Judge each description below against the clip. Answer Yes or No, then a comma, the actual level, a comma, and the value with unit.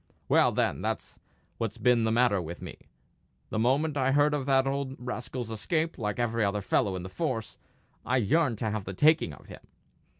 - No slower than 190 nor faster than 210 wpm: Yes, average, 195 wpm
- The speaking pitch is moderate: No, low, 125 Hz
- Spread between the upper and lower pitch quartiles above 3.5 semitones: Yes, average, 4.2 semitones